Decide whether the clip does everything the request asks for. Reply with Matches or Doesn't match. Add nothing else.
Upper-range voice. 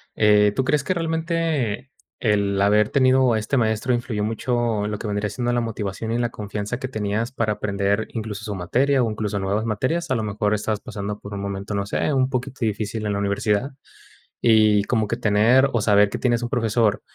Doesn't match